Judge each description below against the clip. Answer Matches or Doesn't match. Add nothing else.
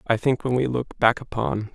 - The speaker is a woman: Doesn't match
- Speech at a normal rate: Doesn't match